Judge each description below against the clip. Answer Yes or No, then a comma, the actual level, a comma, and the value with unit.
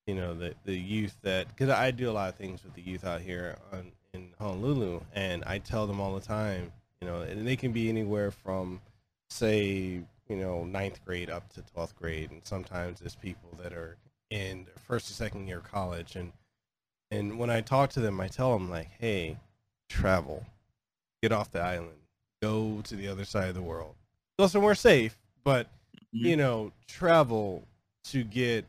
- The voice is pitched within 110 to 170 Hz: No, low, 100 Hz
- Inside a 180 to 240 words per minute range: Yes, average, 190 wpm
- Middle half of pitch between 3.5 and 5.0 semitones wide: Yes, average, 4.0 semitones